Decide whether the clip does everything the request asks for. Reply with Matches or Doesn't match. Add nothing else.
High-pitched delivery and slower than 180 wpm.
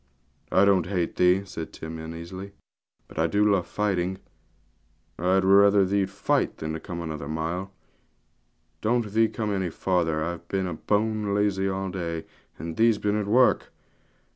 Doesn't match